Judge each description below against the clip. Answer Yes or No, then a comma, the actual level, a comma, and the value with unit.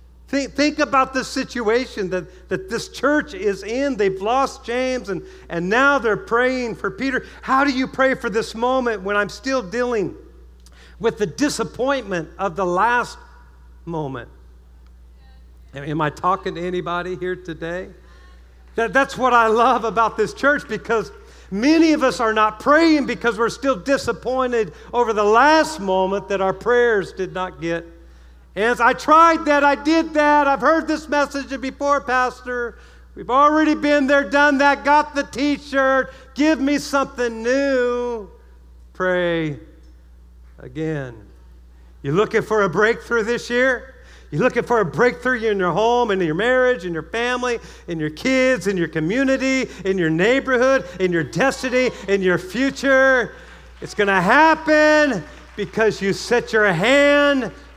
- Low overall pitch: No, high, 235 Hz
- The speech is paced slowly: No, average, 155 wpm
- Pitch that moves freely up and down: Yes, wide, 6.5 semitones